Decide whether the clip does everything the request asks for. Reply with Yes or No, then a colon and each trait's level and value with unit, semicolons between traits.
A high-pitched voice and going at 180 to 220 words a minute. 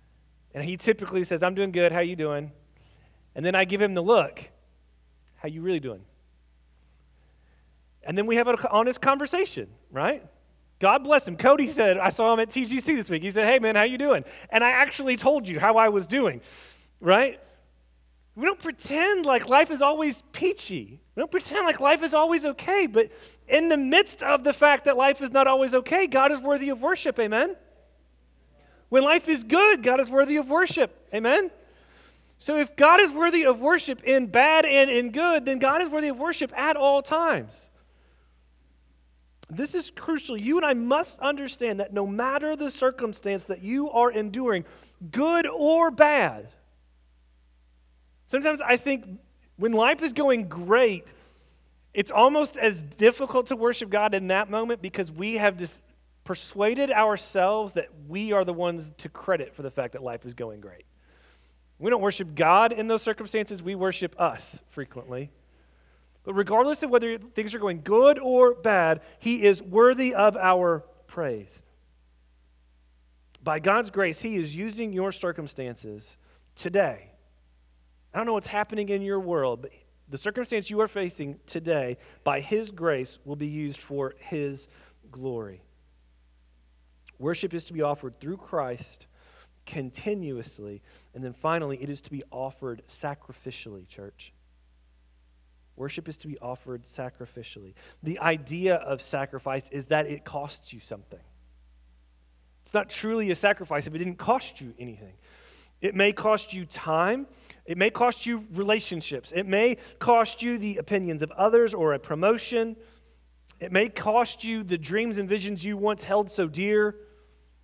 No: high, 195 Hz; average, 165 wpm